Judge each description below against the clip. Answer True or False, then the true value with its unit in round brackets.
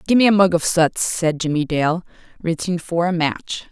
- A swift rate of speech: False (195 wpm)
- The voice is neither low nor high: True (170 Hz)